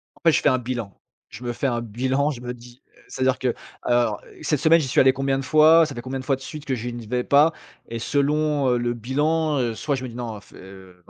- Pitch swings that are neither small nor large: Yes, average, 3.1 semitones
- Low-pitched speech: Yes, low, 130 Hz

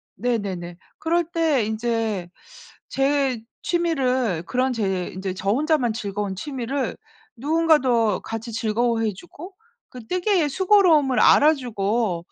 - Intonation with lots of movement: Yes, wide, 6.0 semitones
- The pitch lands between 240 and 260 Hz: Yes, high, 245 Hz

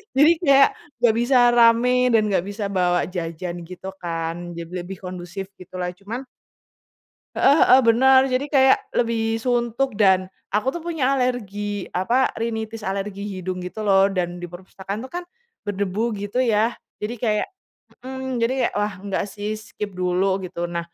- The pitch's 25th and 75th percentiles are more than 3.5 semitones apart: Yes, average, 4.6 semitones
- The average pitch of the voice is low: No, high, 205 Hz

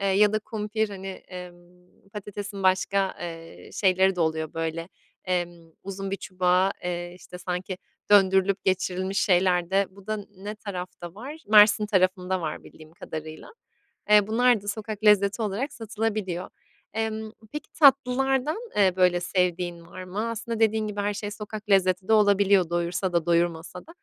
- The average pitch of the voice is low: No, high, 195 Hz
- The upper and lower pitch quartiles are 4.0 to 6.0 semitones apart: No, average, 2.8 semitones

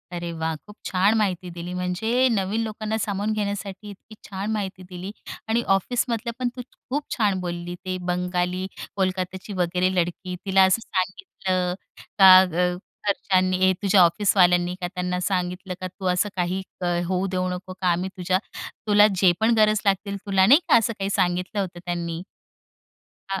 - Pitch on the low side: No, medium, 185 Hz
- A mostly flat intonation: Yes, narrow, 2.2 semitones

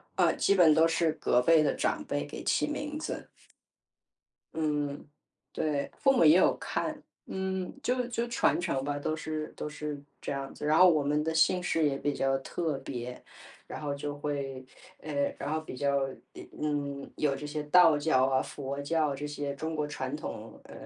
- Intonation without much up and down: Yes, narrow, 2.3 semitones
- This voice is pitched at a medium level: Yes, medium, 150 Hz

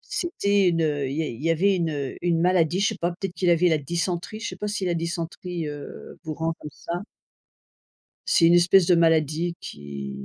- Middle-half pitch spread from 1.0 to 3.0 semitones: Yes, narrow, 2.6 semitones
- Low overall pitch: No, medium, 170 Hz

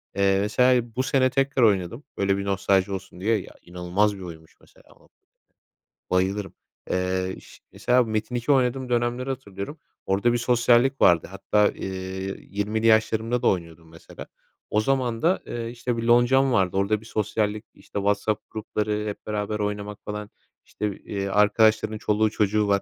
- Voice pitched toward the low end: Yes, low, 105 Hz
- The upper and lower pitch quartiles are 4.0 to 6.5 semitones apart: No, average, 3.3 semitones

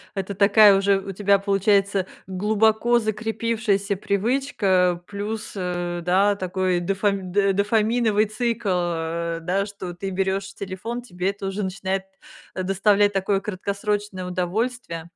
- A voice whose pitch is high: Yes, high, 195 Hz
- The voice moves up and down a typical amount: No, narrow, 2.1 semitones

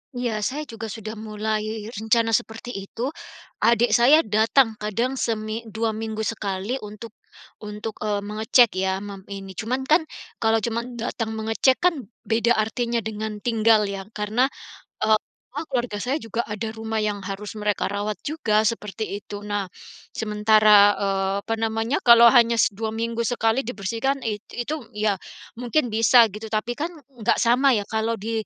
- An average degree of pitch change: No, narrow, 2.0 semitones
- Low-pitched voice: No, high, 220 Hz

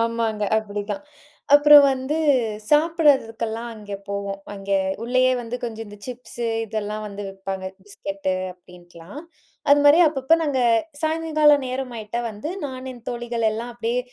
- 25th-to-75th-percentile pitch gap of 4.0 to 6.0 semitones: Yes, average, 4.3 semitones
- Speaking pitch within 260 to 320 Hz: No, high, 230 Hz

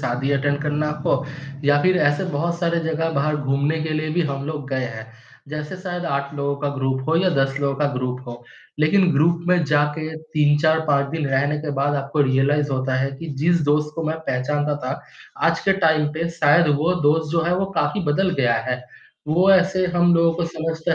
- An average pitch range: Yes, average, 3.0 semitones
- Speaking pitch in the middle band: Yes, medium, 150 Hz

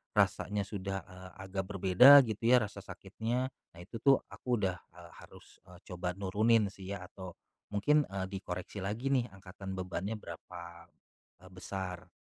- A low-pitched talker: Yes, low, 100 Hz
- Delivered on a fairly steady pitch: No, average, 3.1 semitones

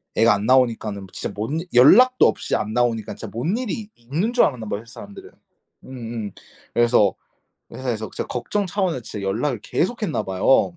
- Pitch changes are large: Yes, wide, 7.4 semitones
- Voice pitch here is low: Yes, low, 120 Hz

